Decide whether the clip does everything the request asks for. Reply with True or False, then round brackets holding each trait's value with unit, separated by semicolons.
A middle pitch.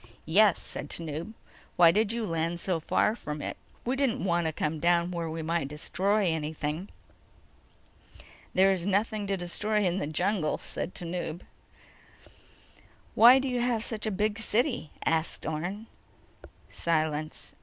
True (180 Hz)